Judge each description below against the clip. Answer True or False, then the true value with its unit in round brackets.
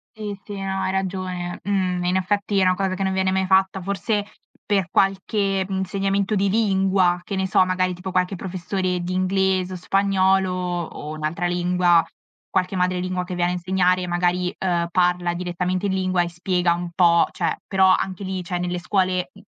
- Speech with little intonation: True (1.3 semitones)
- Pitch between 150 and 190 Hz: True (185 Hz)